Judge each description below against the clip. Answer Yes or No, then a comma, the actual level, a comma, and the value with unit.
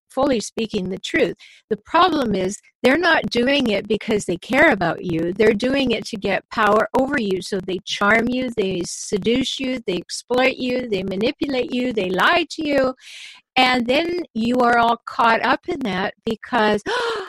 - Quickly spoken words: No, average, 175 wpm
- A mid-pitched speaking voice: No, high, 235 Hz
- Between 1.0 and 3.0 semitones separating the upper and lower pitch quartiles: No, average, 4.2 semitones